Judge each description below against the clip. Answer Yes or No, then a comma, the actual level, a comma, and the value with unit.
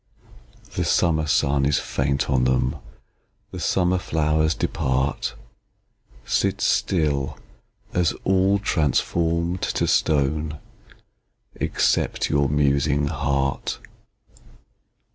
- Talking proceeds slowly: Yes, slow, 85 wpm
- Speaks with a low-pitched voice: Yes, very low, 75 Hz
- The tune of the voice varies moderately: Yes, average, 3.1 semitones